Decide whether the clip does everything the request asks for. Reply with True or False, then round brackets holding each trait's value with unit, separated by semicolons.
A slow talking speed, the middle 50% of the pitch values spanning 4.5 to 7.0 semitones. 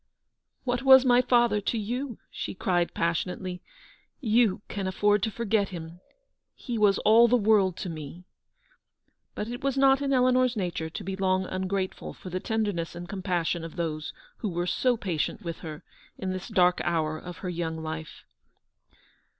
False (175 wpm; 5.1 semitones)